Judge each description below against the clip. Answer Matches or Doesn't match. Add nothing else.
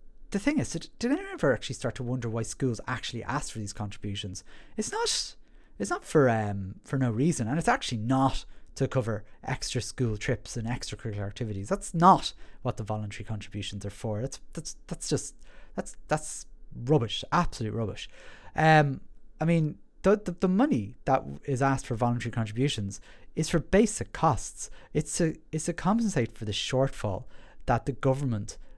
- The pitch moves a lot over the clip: Matches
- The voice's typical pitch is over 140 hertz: Doesn't match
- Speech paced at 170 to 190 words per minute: Matches